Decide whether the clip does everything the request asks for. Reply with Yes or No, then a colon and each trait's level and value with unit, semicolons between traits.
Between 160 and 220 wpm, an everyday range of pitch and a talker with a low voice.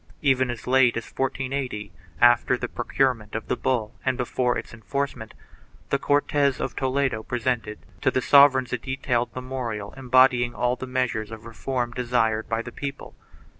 No: average, 170 wpm; narrow, 2.3 semitones; low, 125 Hz